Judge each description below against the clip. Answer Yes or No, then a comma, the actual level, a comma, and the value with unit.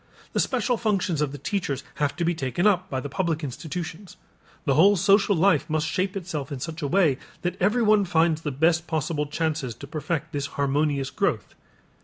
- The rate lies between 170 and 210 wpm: Yes, average, 190 wpm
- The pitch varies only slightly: No, average, 4.4 semitones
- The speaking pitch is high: No, medium, 160 Hz